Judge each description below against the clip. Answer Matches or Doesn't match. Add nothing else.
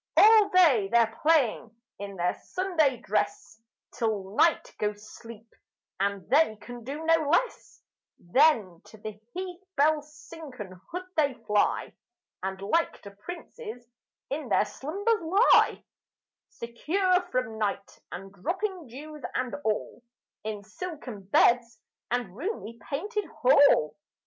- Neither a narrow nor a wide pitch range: Doesn't match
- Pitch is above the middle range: Matches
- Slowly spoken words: Matches